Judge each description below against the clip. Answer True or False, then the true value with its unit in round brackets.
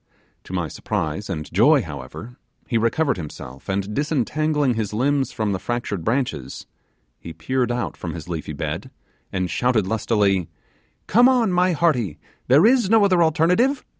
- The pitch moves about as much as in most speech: False (8.5 semitones)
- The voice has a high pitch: False (120 Hz)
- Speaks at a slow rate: False (155 wpm)